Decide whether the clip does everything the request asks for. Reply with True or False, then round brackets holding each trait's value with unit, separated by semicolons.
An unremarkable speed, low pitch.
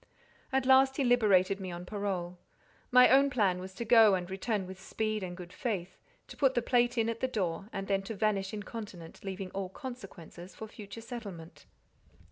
False (195 wpm; 200 Hz)